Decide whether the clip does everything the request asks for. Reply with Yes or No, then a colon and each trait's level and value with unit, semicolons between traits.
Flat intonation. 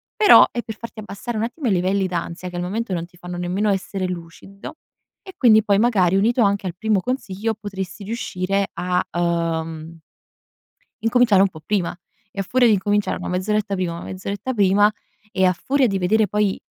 No: average, 3.1 semitones